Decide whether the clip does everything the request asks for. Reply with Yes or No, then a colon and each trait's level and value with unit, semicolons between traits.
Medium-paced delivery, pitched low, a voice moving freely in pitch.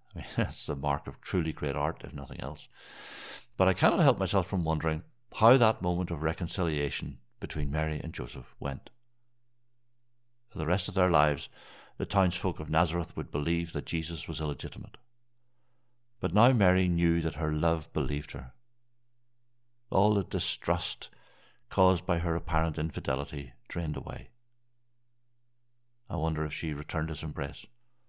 Yes: average, 150 wpm; very low, 90 Hz; wide, 7.4 semitones